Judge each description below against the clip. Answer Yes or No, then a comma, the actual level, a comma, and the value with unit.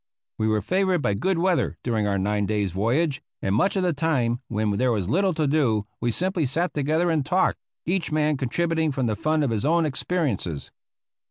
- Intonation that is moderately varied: No, wide, 7.5 semitones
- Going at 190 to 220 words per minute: Yes, average, 200 wpm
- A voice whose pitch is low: No, medium, 145 Hz